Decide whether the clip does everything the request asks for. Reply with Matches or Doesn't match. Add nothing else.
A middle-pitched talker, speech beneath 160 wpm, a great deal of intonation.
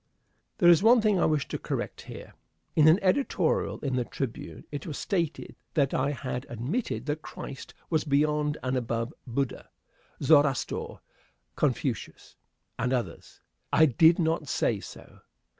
Doesn't match